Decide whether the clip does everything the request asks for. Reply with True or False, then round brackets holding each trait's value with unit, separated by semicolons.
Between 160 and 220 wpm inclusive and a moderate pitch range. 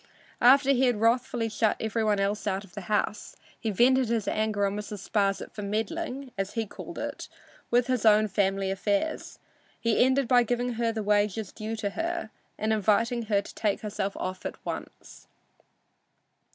True (170 wpm; 3.0 semitones)